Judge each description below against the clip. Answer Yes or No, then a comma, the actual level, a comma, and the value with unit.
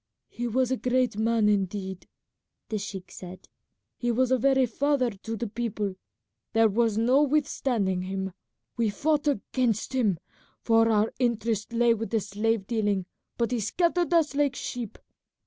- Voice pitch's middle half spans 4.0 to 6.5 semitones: No, average, 3.6 semitones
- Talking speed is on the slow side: No, average, 155 wpm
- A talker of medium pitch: No, high, 230 Hz